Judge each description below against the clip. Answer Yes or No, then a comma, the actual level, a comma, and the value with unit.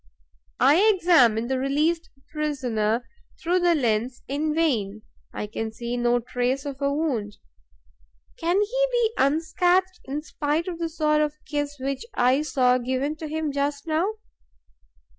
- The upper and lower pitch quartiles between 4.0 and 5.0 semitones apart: Yes, average, 4.6 semitones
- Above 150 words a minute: No, average, 145 wpm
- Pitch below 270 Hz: No, very high, 290 Hz